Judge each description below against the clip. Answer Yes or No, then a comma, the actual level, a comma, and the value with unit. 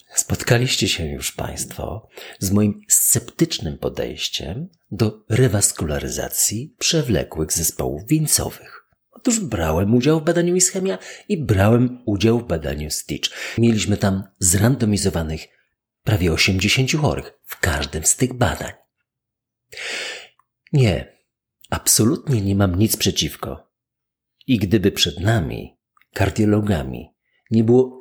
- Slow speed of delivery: Yes, slow, 105 wpm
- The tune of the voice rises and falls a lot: Yes, wide, 5.7 semitones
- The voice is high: No, low, 105 Hz